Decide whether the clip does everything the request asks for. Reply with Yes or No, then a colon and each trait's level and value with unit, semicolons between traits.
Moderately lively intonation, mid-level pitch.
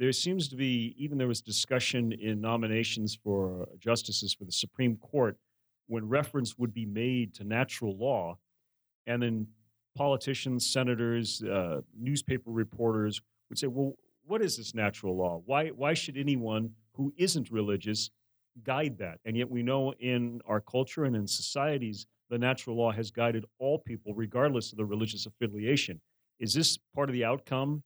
No: average, 3.3 semitones; low, 115 Hz